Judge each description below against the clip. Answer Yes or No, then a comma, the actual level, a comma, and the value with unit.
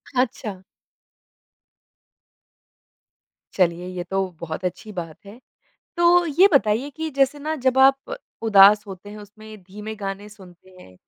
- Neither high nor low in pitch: No, high, 210 Hz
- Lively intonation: Yes, wide, 5.9 semitones